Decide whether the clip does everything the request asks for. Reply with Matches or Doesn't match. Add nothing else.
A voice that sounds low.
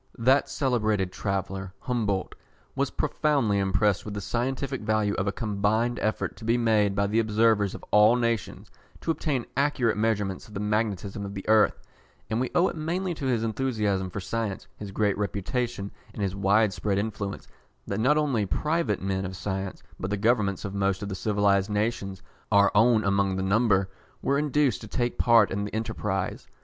Matches